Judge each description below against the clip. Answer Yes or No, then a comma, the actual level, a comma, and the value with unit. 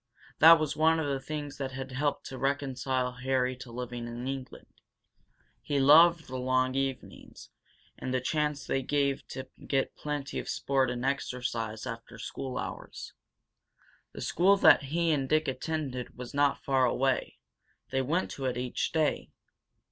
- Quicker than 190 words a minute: No, average, 160 wpm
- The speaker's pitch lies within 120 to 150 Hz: Yes, low, 135 Hz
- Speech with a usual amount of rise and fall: No, narrow, 2.3 semitones